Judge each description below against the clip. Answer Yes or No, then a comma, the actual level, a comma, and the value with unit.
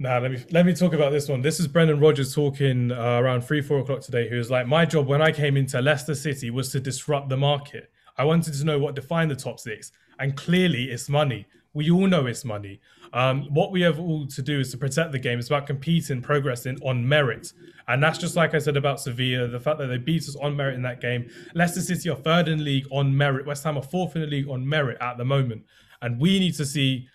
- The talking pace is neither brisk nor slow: No, fast, 255 wpm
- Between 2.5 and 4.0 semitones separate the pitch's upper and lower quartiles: Yes, average, 3.4 semitones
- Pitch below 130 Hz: No, medium, 140 Hz